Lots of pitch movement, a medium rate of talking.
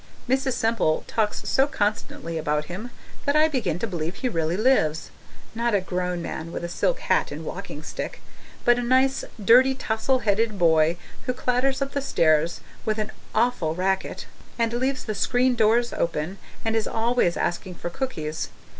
Yes: wide, 6.5 semitones; average, 170 wpm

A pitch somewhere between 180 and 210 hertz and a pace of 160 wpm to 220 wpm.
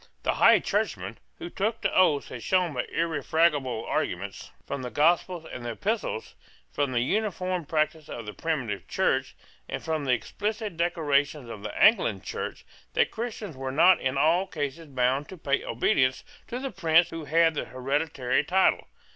No: medium, 155 Hz; average, 170 wpm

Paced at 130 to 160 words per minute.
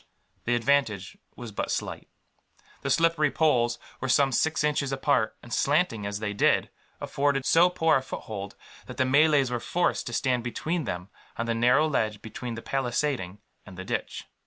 No: average, 175 wpm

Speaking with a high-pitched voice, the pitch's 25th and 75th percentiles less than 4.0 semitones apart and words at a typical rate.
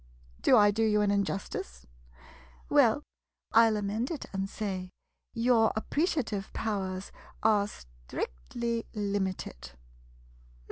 No: high, 205 Hz; average, 2.9 semitones; slow, 110 wpm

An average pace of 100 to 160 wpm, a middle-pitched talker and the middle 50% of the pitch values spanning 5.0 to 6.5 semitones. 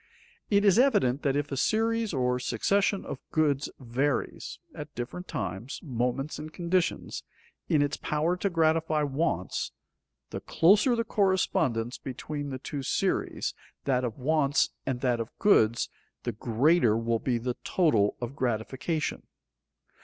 Yes: average, 145 wpm; medium, 145 Hz; wide, 5.4 semitones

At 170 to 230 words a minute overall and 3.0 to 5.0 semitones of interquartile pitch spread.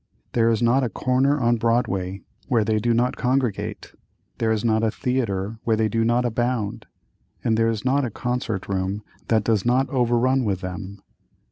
No: average, 180 wpm; narrow, 2.6 semitones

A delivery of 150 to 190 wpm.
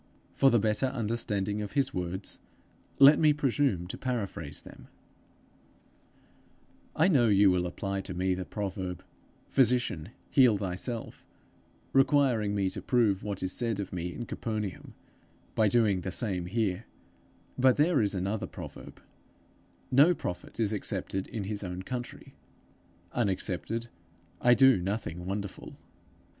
No: slow, 135 wpm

